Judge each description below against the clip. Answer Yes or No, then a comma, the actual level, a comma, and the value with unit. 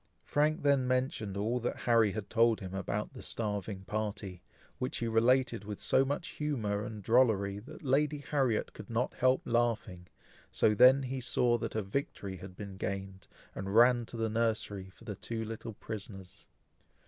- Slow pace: No, average, 170 wpm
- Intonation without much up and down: No, average, 4.0 semitones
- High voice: No, low, 115 Hz